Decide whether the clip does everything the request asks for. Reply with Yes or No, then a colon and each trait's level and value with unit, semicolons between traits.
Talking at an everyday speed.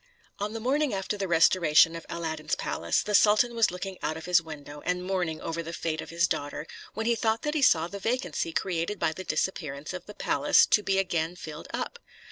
No: fast, 220 wpm